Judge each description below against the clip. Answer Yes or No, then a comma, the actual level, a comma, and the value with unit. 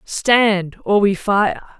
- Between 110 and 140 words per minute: Yes, slow, 135 wpm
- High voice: Yes, high, 200 Hz